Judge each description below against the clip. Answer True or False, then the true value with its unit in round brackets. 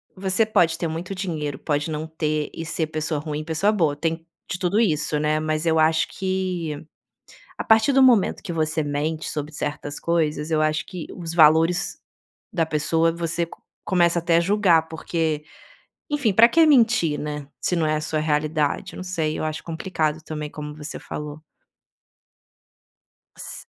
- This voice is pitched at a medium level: True (160 Hz)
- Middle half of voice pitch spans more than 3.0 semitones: False (2.6 semitones)